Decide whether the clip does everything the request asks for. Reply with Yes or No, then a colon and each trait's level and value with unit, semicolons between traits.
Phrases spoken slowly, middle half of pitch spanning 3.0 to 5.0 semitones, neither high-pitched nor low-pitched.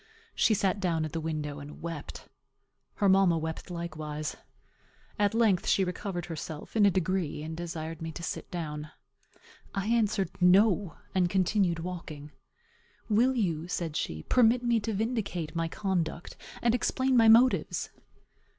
No: average, 150 wpm; average, 4.3 semitones; medium, 180 Hz